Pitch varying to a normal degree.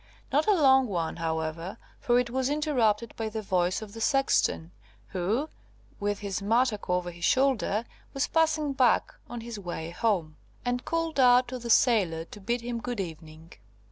No: wide, 6.2 semitones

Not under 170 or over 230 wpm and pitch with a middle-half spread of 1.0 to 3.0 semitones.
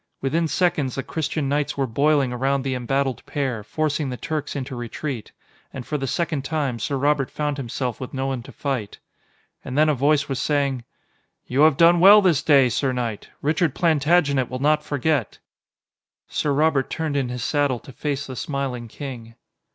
Yes: average, 180 wpm; average, 2.7 semitones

